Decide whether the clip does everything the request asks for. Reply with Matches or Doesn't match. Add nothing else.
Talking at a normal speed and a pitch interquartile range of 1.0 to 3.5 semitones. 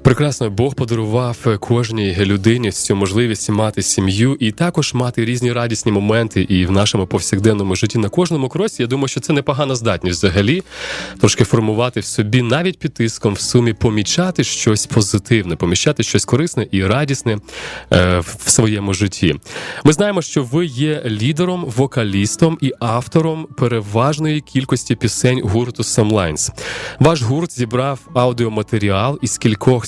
Doesn't match